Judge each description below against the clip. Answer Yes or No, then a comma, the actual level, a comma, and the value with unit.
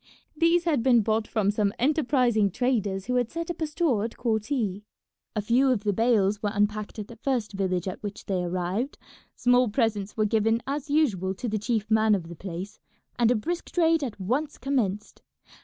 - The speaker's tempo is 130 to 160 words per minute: No, average, 195 wpm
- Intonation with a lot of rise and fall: No, average, 4.1 semitones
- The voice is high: Yes, high, 220 Hz